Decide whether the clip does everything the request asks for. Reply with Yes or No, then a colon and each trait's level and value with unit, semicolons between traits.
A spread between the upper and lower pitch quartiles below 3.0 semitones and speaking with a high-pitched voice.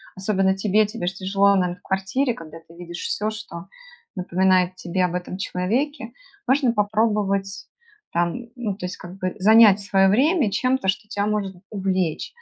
Yes: narrow, 2.6 semitones; high, 195 Hz